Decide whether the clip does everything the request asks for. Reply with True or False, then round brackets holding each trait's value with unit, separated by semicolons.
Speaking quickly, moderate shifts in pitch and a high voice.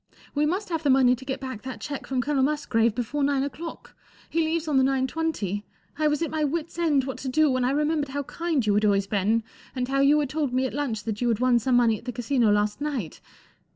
True (255 wpm; 3.7 semitones; 265 Hz)